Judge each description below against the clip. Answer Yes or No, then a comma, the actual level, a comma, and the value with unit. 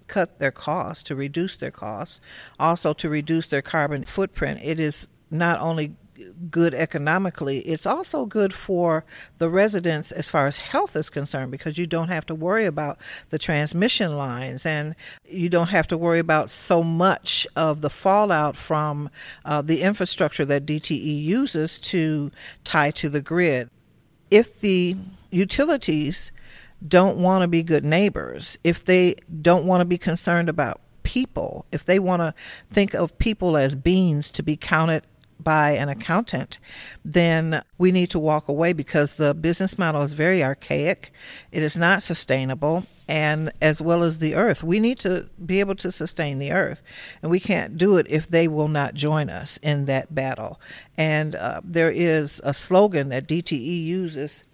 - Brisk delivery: No, average, 170 wpm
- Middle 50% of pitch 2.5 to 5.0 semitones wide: Yes, average, 3.2 semitones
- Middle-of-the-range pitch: Yes, medium, 160 Hz